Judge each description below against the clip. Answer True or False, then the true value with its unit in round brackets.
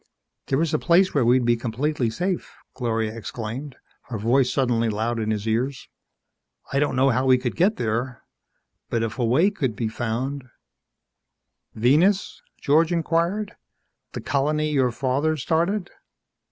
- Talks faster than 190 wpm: False (155 wpm)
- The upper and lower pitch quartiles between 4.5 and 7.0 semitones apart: True (4.9 semitones)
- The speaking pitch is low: True (130 Hz)